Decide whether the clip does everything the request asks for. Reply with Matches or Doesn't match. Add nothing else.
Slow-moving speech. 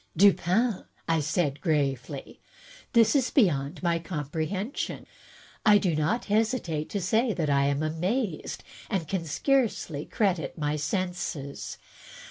Matches